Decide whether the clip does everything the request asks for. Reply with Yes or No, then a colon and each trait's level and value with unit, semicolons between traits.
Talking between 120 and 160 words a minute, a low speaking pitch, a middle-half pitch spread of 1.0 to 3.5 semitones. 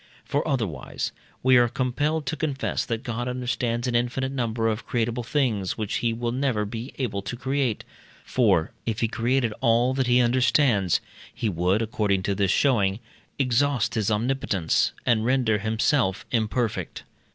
Yes: average, 155 wpm; low, 120 Hz; average, 3.1 semitones